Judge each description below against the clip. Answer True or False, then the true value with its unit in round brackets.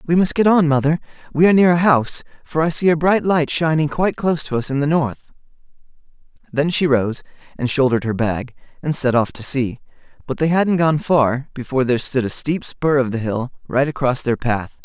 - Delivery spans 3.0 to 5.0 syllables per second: False (5.8 syllables/s)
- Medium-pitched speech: True (145 Hz)